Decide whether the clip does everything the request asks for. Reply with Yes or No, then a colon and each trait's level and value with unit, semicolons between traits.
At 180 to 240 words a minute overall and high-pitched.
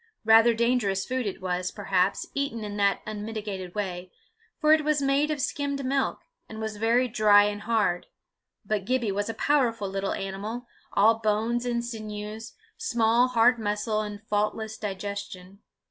No: average, 155 wpm; high, 215 Hz